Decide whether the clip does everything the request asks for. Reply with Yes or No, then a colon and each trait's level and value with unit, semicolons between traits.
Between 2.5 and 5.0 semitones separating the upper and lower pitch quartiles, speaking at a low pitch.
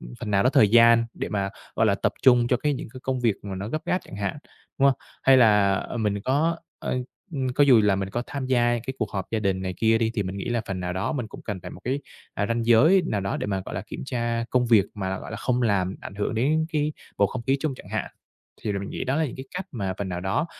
Yes: average, 4.7 semitones; low, 115 Hz